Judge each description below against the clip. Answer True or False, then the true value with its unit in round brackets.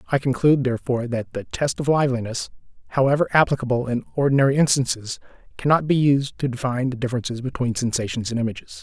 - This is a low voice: True (130 Hz)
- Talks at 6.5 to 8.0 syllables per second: True (7.0 syllables/s)